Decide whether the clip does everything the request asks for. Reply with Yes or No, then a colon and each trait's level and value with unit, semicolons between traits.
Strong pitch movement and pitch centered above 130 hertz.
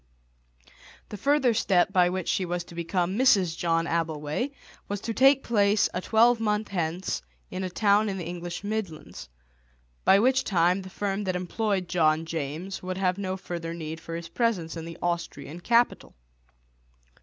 No: average, 3.6 semitones; medium, 185 Hz